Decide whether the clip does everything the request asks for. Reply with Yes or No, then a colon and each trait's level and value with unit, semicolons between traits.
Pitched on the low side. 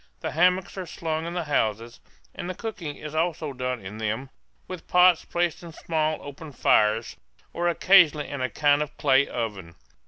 No: medium, 150 Hz